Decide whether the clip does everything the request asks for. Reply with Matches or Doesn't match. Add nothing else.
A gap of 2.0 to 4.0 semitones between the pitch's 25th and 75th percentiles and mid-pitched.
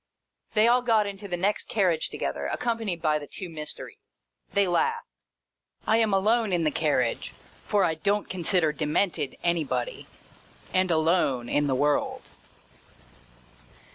Doesn't match